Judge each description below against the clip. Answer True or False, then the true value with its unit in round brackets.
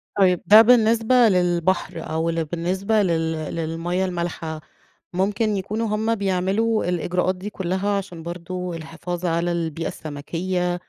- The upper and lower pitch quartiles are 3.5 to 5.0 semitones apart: False (3.1 semitones)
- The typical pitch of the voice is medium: True (180 Hz)